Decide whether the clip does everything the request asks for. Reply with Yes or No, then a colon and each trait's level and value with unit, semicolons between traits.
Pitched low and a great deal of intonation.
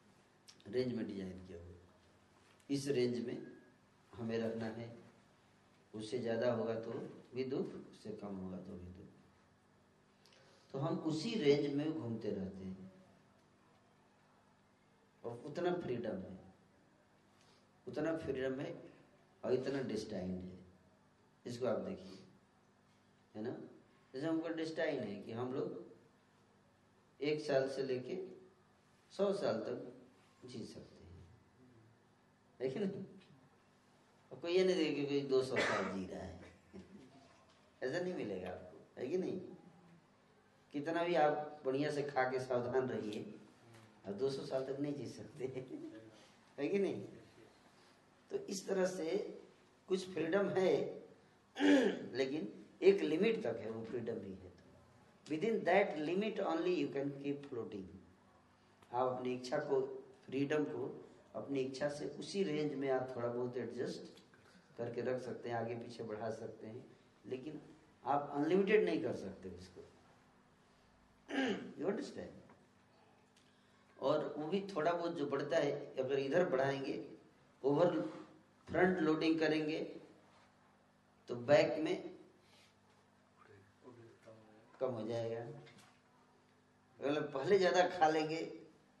Yes: low, 130 Hz; wide, 5.7 semitones